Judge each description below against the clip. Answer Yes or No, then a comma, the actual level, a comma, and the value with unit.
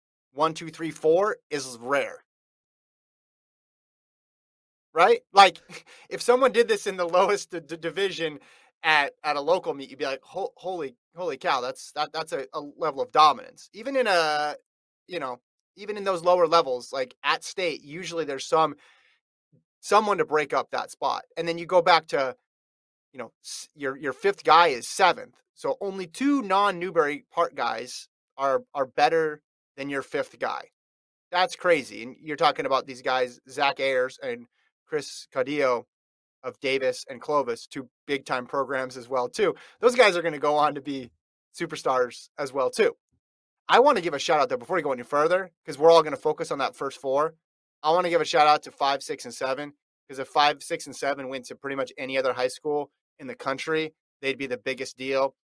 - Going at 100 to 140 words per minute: No, average, 195 wpm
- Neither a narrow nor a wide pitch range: No, wide, 5.7 semitones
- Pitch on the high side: No, medium, 155 Hz